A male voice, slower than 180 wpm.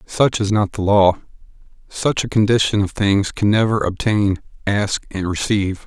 Yes: male; average, 165 wpm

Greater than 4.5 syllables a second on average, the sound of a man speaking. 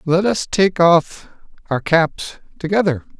No: 3.6 syllables/s; male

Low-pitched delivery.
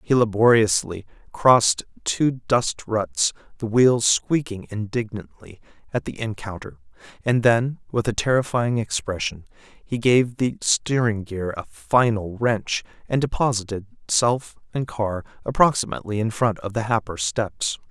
Yes: low, 110 Hz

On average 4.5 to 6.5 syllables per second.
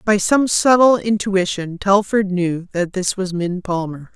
No: 4.0 syllables/s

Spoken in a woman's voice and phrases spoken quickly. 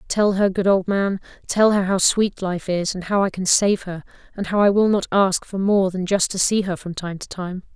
Yes: female; fast, 265 wpm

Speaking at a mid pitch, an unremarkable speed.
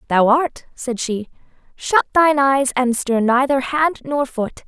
No: very high, 265 Hz; average, 165 wpm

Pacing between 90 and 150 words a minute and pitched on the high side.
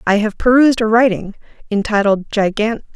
Yes: average, 140 wpm; high, 220 Hz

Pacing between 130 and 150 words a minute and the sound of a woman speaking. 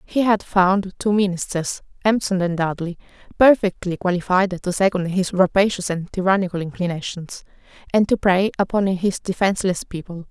Yes: average, 140 wpm; female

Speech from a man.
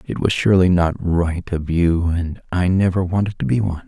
Yes: male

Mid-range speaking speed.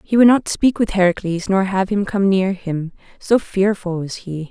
No: fast, 215 wpm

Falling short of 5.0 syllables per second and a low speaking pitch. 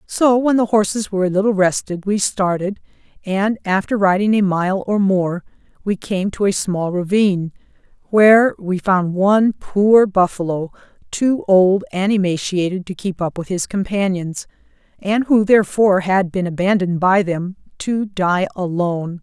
No: 4.6 syllables/s; high, 190 Hz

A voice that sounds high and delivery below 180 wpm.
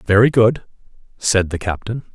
No: low, 110 Hz; average, 140 wpm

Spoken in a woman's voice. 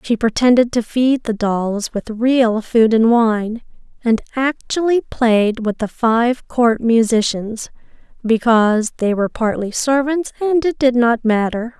Yes: female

